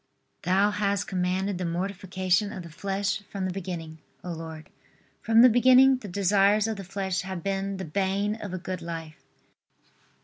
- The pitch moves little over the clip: Yes, narrow, 2.1 semitones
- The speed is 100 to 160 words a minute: No, average, 170 wpm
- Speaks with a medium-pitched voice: No, high, 195 Hz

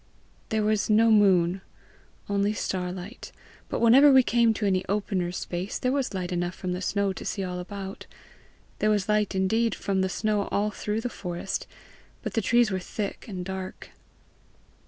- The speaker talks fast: No, average, 175 wpm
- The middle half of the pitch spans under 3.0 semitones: Yes, narrow, 2.6 semitones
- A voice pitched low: No, high, 200 Hz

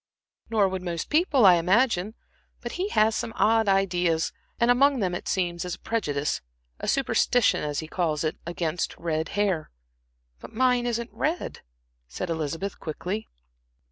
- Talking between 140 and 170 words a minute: Yes, average, 155 wpm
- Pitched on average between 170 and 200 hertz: Yes, high, 190 Hz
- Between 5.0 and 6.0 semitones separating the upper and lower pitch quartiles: Yes, wide, 5.6 semitones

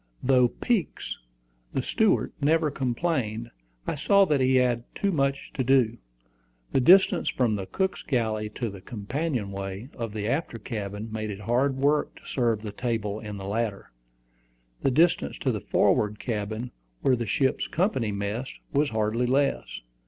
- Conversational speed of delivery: Yes, average, 160 wpm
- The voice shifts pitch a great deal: No, average, 4.4 semitones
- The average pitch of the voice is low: Yes, low, 120 Hz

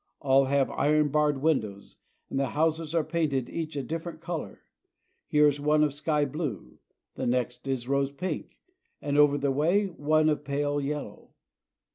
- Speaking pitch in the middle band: Yes, medium, 145 Hz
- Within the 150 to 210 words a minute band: Yes, average, 175 wpm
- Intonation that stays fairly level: Yes, narrow, 2.2 semitones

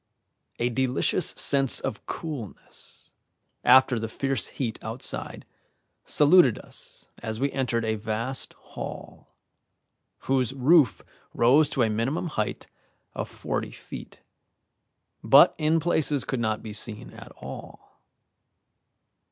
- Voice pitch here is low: Yes, low, 130 Hz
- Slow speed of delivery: Yes, slow, 115 wpm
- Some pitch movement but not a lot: Yes, average, 4.0 semitones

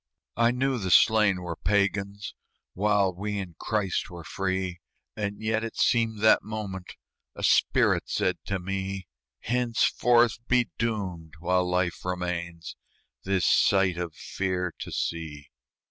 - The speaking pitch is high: No, very low, 95 Hz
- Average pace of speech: No, slow, 130 wpm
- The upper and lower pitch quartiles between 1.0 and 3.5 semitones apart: Yes, average, 3.2 semitones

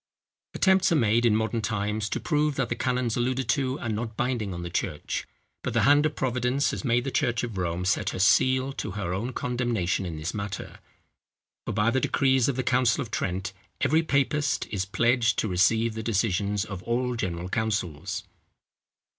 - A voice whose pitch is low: Yes, low, 115 Hz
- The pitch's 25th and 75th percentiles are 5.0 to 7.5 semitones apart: No, average, 4.2 semitones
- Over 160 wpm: Yes, average, 190 wpm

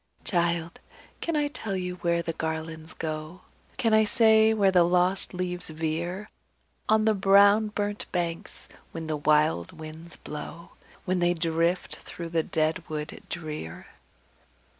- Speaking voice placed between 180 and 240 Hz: No, medium, 170 Hz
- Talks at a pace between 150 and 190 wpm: No, average, 140 wpm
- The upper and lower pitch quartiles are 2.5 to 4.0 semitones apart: Yes, average, 3.5 semitones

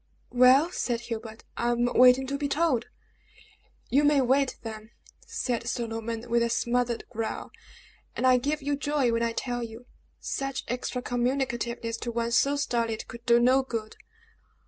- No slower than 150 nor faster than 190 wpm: Yes, average, 165 wpm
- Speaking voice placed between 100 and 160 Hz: No, high, 245 Hz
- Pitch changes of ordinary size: No, narrow, 2.3 semitones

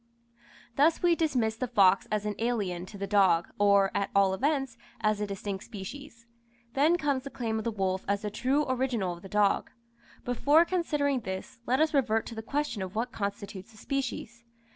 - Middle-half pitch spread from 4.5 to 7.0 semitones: Yes, average, 5.2 semitones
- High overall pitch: Yes, high, 225 Hz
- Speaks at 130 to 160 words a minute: No, average, 190 wpm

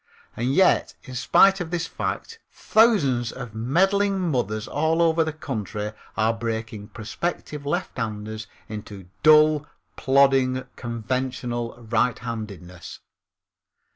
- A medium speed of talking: No, slow, 105 wpm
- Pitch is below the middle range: Yes, low, 125 Hz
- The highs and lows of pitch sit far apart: Yes, wide, 5.9 semitones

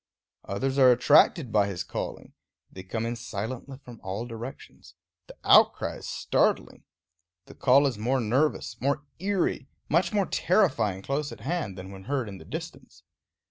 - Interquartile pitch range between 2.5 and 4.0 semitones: No, average, 5.1 semitones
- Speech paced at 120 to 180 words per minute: Yes, average, 160 wpm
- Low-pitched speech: Yes, low, 125 Hz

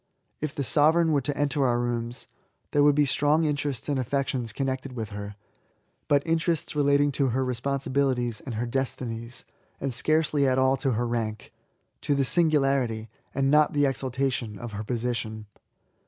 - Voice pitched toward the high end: No, low, 135 Hz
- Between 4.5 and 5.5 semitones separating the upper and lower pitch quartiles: No, average, 3.2 semitones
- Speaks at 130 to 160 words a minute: No, average, 175 wpm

